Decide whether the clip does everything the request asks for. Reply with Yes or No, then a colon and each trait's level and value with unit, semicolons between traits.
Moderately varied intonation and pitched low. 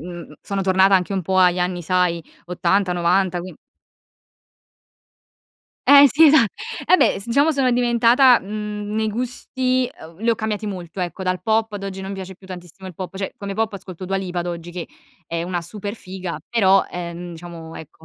No: average, 3.6 semitones; high, 190 Hz